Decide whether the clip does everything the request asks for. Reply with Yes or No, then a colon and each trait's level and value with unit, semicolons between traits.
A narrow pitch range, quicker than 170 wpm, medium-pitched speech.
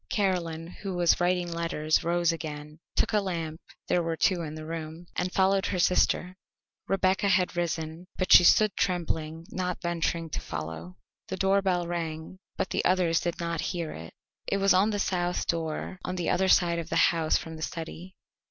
Yes: narrow, 2.3 semitones; average, 185 wpm; medium, 175 Hz